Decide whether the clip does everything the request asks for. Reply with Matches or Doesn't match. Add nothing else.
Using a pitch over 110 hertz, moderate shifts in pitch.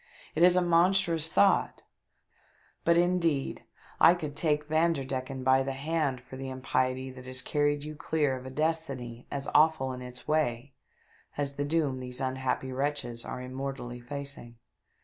Matches